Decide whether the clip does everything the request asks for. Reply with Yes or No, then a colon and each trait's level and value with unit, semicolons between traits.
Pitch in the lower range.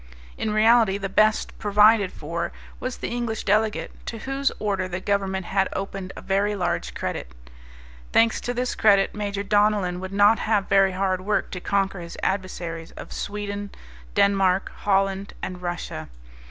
No: high, 200 Hz